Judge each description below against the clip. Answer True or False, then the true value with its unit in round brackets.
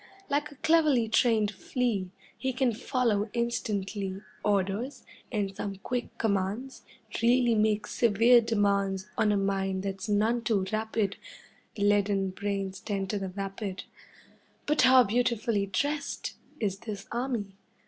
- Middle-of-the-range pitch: False (210 Hz)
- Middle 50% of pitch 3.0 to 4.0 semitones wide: True (3.4 semitones)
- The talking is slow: True (130 wpm)